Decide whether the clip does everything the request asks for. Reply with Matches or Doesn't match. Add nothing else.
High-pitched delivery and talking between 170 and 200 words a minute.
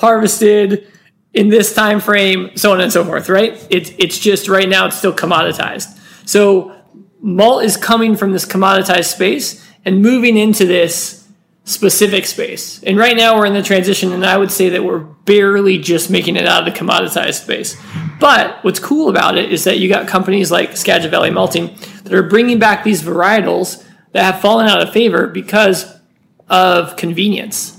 Matches